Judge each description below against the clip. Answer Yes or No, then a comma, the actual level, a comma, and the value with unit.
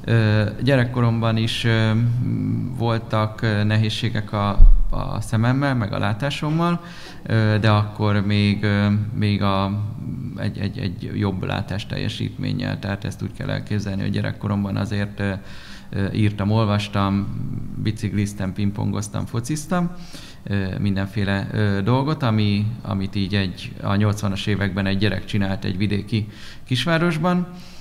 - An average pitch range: Yes, average, 3.3 semitones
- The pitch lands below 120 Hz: Yes, low, 105 Hz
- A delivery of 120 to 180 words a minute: No, slow, 105 wpm